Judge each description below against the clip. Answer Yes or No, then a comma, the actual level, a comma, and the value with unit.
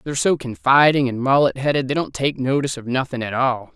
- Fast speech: Yes, fast, 225 wpm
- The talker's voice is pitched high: No, low, 135 Hz